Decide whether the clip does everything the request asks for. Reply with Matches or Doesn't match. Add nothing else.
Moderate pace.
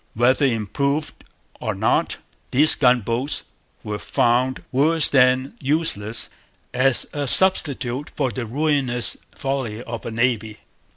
Doesn't match